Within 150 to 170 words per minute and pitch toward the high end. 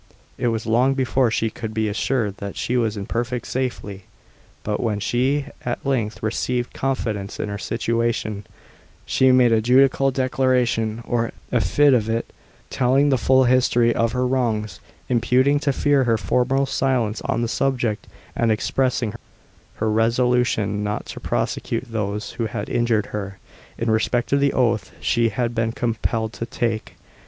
No: average, 155 wpm; low, 120 Hz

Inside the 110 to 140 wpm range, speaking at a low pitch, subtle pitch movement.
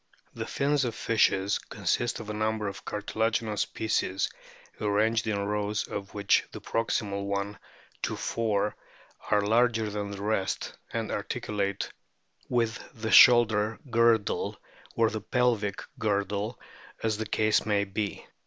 Yes: slow, 135 wpm; low, 105 Hz; narrow, 1.8 semitones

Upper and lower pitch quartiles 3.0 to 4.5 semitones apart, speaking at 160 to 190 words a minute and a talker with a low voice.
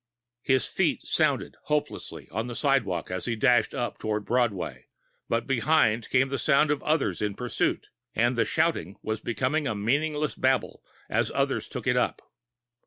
Yes: average, 4.1 semitones; average, 165 wpm; low, 120 Hz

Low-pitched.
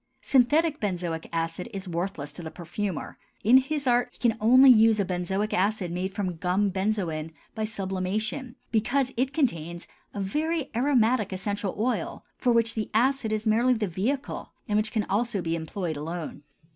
No: high, 210 Hz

